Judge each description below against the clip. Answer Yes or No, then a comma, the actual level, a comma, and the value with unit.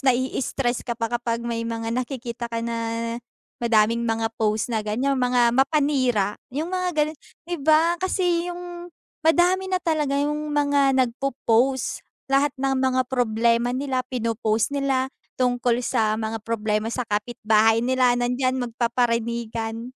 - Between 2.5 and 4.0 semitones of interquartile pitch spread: Yes, average, 3.2 semitones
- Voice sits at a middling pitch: No, high, 245 Hz